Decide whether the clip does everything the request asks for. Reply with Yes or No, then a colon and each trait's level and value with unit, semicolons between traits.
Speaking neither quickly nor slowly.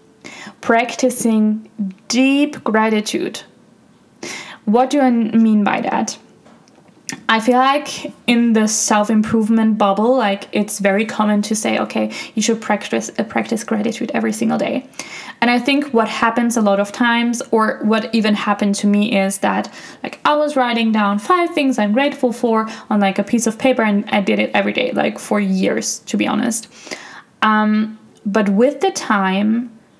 Yes: average, 165 wpm